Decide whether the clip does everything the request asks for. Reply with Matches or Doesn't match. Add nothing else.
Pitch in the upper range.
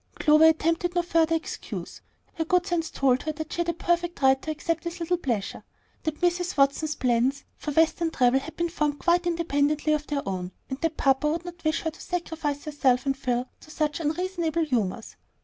Matches